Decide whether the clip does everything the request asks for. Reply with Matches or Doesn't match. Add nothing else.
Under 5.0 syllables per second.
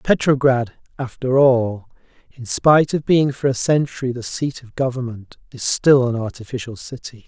Matches